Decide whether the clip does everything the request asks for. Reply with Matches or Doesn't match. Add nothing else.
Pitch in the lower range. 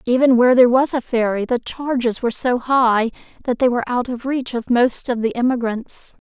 Doesn't match